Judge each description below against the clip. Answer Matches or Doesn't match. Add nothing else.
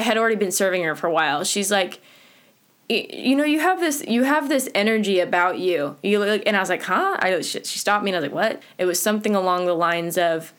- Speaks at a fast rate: Matches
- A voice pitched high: Matches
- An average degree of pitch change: Matches